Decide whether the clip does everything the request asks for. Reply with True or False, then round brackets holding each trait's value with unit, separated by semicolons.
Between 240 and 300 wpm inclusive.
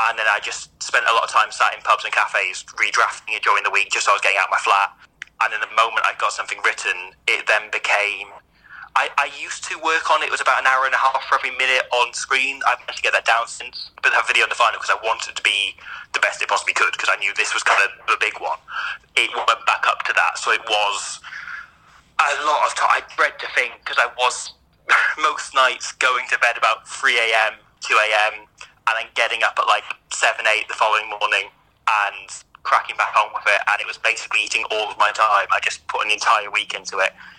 True (255 wpm)